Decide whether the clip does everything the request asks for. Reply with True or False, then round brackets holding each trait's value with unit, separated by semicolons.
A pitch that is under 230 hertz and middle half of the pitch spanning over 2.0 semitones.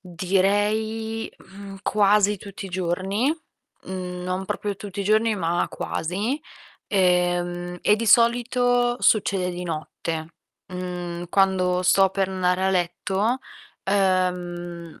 True (190 Hz; 2.6 semitones)